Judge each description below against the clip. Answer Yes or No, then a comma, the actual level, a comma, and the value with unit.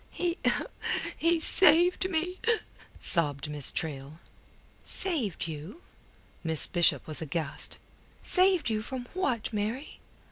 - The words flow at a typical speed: No, slow, 105 wpm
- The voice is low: No, high, 220 Hz